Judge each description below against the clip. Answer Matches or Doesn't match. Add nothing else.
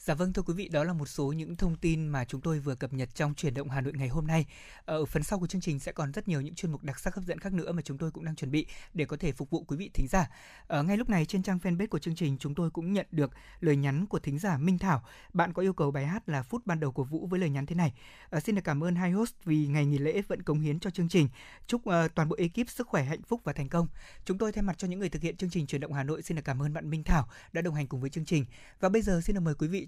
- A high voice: Doesn't match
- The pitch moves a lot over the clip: Doesn't match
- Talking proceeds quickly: Matches